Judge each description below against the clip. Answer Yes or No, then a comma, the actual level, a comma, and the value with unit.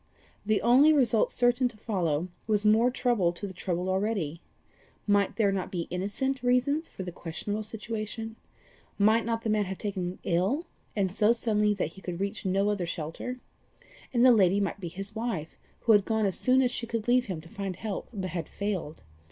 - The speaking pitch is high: Yes, high, 205 Hz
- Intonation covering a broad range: No, average, 3.7 semitones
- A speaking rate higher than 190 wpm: Yes, average, 200 wpm